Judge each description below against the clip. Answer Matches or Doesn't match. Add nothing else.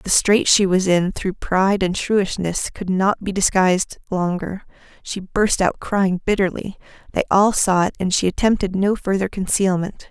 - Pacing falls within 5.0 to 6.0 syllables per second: Doesn't match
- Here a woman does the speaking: Matches